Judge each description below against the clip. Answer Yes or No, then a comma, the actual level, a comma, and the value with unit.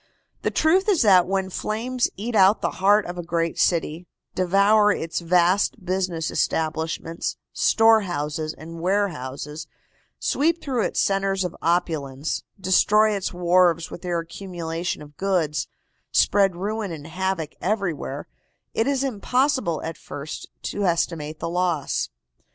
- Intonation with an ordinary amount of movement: Yes, average, 3.7 semitones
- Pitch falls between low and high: Yes, medium, 180 Hz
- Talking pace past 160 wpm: No, slow, 135 wpm